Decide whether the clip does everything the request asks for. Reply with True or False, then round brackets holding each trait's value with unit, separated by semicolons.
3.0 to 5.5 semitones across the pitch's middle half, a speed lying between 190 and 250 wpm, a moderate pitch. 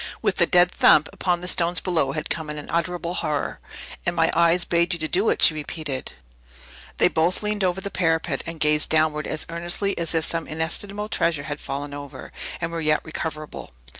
False (2.4 semitones; 195 wpm; 165 Hz)